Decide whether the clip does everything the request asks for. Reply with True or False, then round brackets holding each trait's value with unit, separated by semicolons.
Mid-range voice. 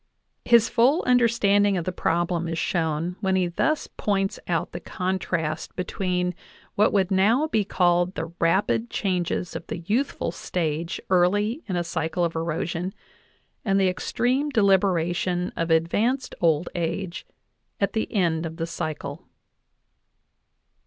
True (180 Hz)